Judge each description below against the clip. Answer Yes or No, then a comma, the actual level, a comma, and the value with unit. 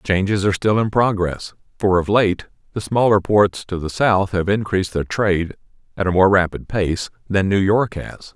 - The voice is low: Yes, low, 100 Hz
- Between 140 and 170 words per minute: No, average, 195 wpm